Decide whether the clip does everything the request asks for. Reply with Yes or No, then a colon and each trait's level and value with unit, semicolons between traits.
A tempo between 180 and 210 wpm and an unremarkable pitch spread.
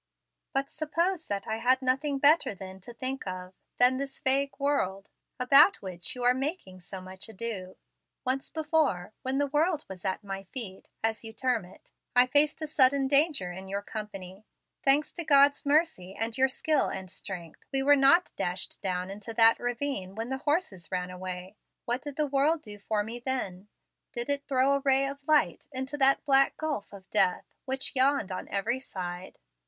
No: average, 190 wpm; wide, 6.5 semitones